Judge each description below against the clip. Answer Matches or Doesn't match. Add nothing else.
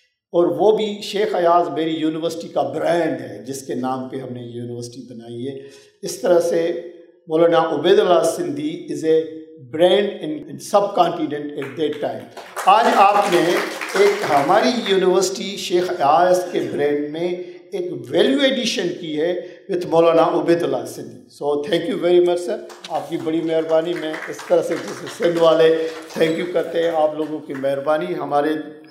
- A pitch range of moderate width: Matches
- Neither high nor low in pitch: Matches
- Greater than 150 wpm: Matches